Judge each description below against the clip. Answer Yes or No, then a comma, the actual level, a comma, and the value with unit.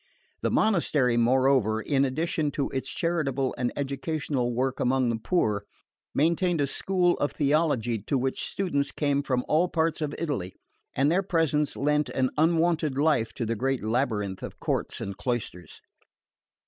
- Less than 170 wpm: Yes, average, 155 wpm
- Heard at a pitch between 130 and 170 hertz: Yes, medium, 140 Hz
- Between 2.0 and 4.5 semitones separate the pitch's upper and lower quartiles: Yes, average, 4.2 semitones